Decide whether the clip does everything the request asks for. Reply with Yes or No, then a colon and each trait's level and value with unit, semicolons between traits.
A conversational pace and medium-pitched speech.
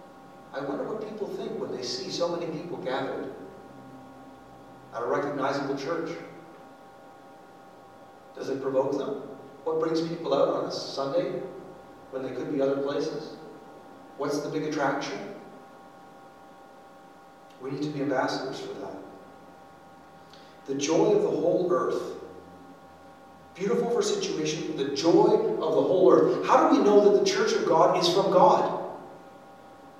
Yes: average, 145 wpm; medium, 155 Hz